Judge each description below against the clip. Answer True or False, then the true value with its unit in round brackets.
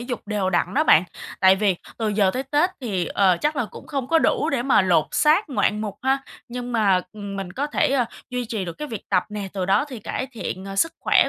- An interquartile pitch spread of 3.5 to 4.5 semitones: False (5.5 semitones)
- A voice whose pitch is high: True (215 Hz)